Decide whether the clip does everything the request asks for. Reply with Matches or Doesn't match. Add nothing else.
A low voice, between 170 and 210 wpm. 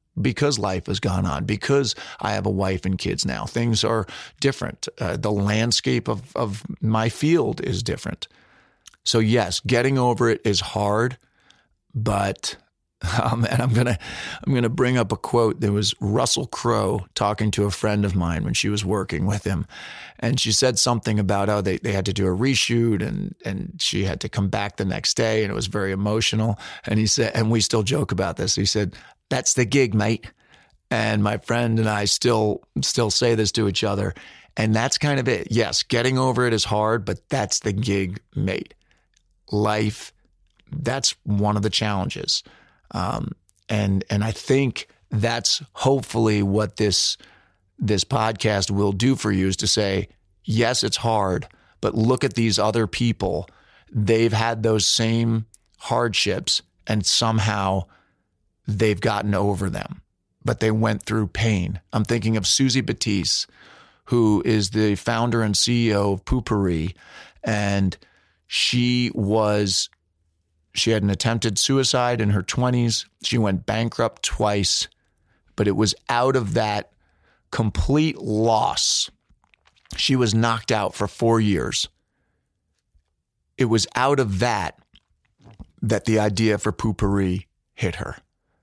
Doesn't match